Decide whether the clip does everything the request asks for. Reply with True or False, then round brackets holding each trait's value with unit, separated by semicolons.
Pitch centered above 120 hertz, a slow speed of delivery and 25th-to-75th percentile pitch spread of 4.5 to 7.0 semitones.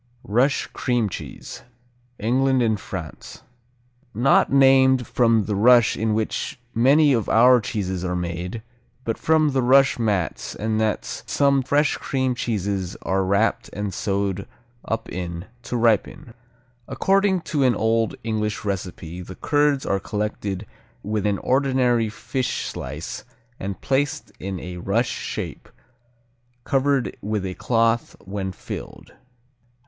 False (110 Hz; 130 wpm; 4.9 semitones)